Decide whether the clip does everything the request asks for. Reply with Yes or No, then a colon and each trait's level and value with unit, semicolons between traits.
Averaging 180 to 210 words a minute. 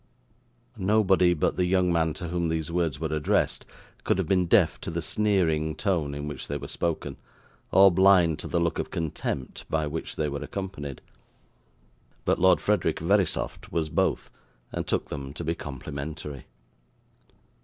No: average, 165 wpm